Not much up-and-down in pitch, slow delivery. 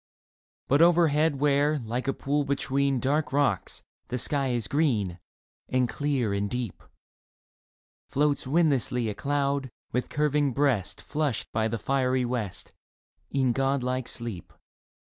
No: average, 3.0 semitones; slow, 130 wpm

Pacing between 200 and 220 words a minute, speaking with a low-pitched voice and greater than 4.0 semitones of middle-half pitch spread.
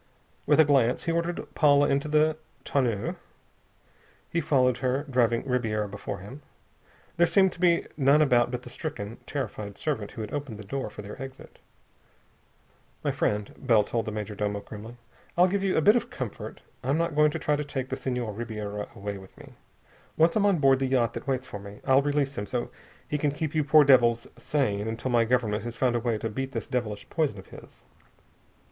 Yes: fast, 205 wpm; low, 130 Hz; average, 5.1 semitones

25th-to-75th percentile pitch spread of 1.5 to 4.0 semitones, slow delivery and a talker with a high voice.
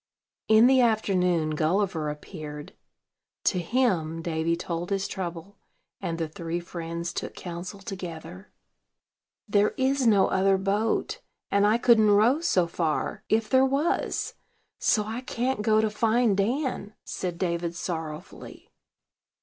No: average, 4.5 semitones; slow, 130 wpm; high, 195 Hz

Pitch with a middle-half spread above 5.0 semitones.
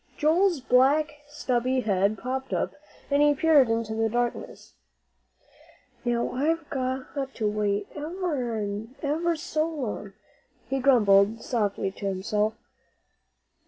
Yes: wide, 5.4 semitones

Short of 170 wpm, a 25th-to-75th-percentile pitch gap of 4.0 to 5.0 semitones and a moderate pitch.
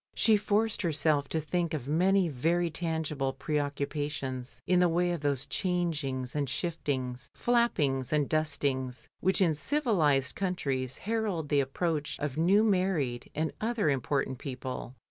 Yes: average, 145 wpm; average, 4.7 semitones; medium, 155 Hz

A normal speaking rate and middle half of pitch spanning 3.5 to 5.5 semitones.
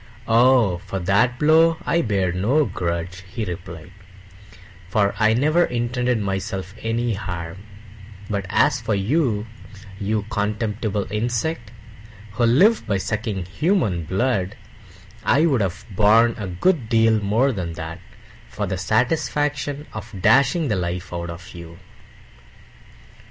No: slow, 125 wpm; average, 5.0 semitones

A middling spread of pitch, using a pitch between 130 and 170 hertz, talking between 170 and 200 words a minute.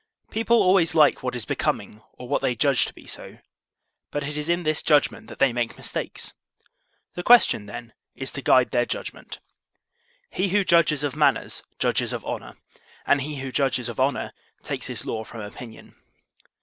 Yes: average, 4.2 semitones; medium, 140 Hz; average, 180 wpm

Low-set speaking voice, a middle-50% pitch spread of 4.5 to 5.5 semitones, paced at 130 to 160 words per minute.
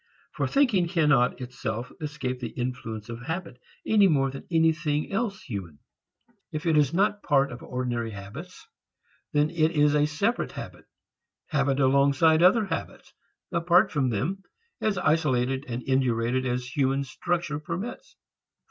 No: medium, 145 Hz; average, 4.9 semitones; average, 145 wpm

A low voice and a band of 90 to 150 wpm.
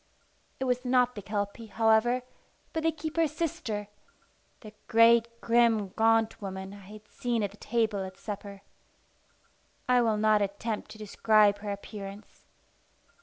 No: high, 220 Hz; average, 140 wpm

